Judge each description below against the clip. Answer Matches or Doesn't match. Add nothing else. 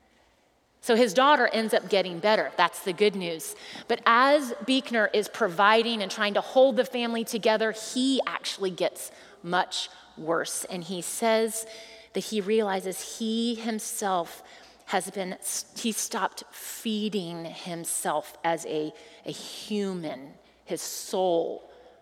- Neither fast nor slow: Doesn't match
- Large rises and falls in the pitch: Doesn't match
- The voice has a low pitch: Doesn't match